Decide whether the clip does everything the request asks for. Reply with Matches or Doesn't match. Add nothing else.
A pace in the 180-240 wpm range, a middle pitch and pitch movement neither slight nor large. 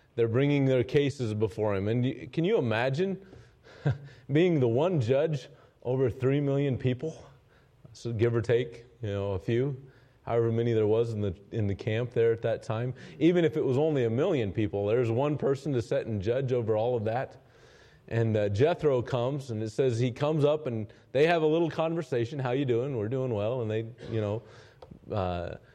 Doesn't match